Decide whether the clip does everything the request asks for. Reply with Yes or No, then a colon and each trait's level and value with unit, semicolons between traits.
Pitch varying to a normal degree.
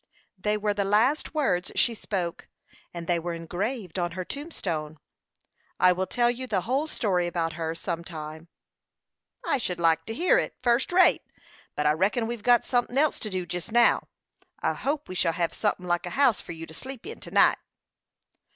No: wide, 6.2 semitones